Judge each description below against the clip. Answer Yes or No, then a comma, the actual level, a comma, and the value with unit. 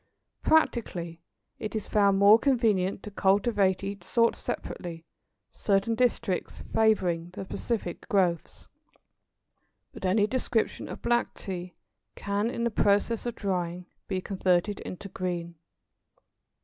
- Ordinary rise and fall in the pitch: Yes, average, 3.5 semitones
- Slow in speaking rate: Yes, slow, 120 wpm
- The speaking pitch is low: No, high, 200 Hz